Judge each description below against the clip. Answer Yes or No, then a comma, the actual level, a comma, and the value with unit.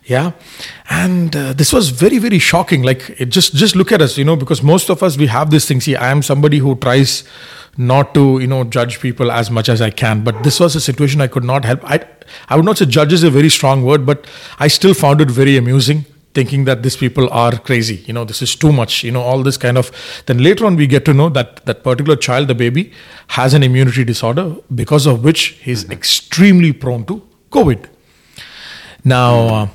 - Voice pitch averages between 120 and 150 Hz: Yes, medium, 140 Hz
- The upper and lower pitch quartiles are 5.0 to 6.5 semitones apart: No, average, 3.5 semitones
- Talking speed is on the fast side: Yes, fast, 230 wpm